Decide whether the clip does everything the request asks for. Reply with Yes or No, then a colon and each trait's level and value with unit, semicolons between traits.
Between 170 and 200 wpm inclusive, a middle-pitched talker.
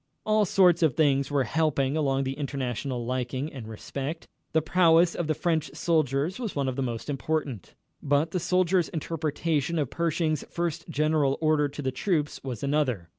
Yes: average, 175 wpm; medium, 150 Hz